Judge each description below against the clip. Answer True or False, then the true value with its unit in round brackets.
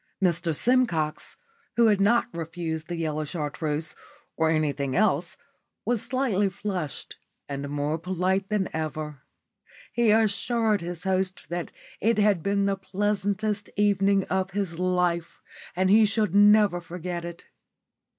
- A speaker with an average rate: False (130 wpm)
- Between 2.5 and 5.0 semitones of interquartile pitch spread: True (4.0 semitones)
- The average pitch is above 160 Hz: True (185 Hz)